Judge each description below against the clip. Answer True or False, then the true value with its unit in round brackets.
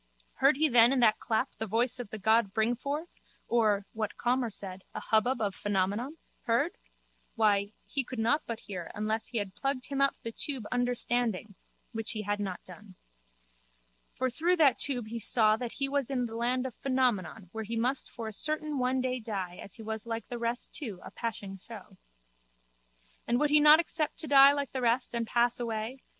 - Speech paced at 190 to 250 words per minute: True (200 wpm)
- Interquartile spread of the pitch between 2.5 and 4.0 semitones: True (3.3 semitones)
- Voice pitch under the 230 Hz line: False (235 Hz)